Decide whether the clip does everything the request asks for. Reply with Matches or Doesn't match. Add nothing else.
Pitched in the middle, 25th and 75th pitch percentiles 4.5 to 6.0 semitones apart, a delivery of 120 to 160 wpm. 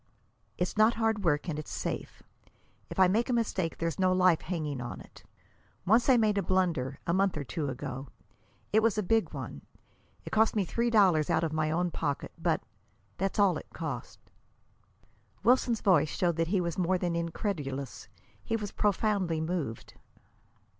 Doesn't match